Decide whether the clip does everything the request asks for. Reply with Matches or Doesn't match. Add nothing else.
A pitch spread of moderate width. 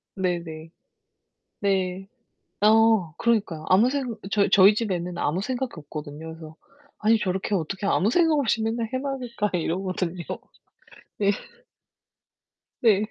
Matches